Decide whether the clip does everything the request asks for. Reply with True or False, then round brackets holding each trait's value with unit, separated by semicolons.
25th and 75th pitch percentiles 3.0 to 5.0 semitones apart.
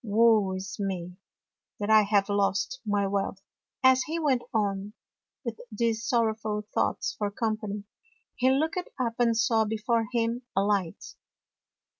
False (2.6 semitones)